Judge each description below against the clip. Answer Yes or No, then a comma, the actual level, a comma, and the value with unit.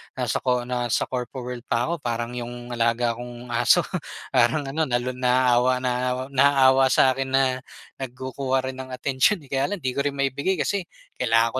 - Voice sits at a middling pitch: No, low, 125 Hz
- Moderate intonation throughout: No, narrow, 1.6 semitones